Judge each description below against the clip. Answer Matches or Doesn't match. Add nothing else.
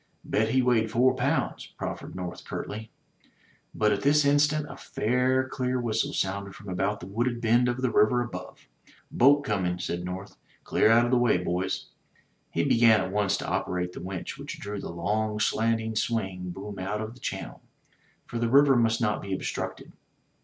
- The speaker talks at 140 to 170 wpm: Doesn't match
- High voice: Doesn't match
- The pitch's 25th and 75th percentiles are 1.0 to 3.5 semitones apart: Doesn't match